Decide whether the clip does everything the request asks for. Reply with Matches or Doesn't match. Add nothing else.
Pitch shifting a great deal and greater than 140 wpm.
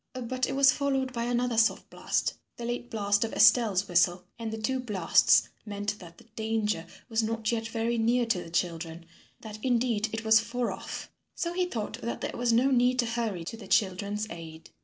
Doesn't match